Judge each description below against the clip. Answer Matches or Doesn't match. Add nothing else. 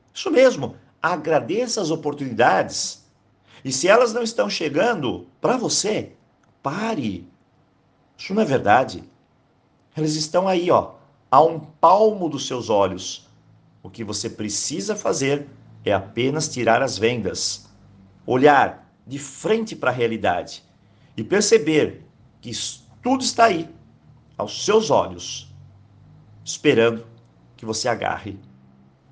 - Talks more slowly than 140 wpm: Matches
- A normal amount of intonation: Doesn't match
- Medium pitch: Doesn't match